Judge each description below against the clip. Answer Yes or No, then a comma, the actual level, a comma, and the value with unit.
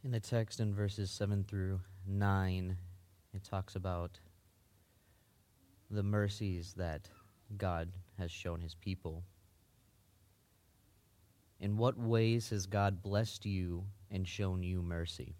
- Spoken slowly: Yes, slow, 115 wpm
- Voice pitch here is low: Yes, very low, 95 Hz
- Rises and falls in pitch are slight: Yes, narrow, 2.0 semitones